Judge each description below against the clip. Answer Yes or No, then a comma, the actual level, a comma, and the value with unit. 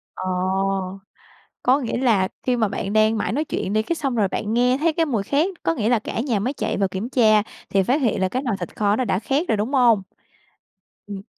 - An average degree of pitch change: Yes, average, 4.2 semitones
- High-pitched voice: Yes, high, 225 Hz